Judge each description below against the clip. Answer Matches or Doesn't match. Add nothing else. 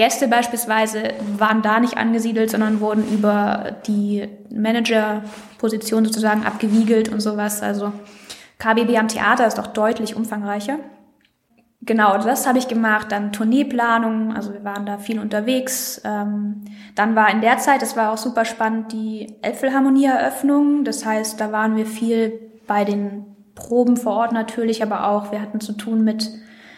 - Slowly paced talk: Doesn't match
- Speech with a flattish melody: Matches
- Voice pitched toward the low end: Doesn't match